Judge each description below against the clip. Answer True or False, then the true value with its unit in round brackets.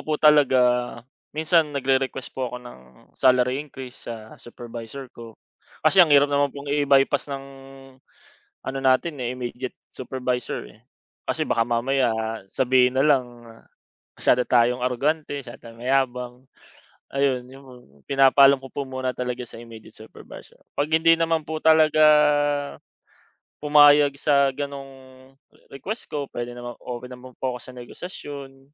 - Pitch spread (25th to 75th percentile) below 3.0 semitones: True (2.4 semitones)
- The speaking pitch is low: True (130 Hz)